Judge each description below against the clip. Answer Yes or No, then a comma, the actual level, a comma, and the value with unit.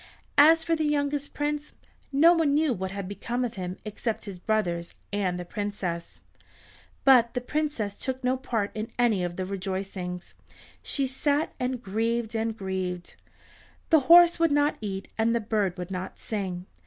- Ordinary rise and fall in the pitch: No, wide, 6.8 semitones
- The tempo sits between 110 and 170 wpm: Yes, average, 165 wpm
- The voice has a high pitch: Yes, high, 220 Hz